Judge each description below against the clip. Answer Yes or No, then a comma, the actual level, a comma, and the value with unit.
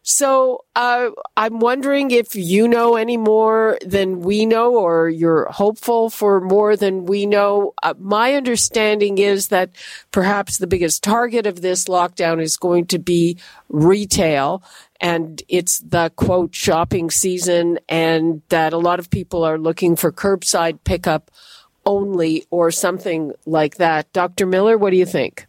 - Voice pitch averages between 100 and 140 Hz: No, medium, 185 Hz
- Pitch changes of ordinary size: Yes, average, 3.9 semitones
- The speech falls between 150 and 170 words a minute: Yes, average, 155 wpm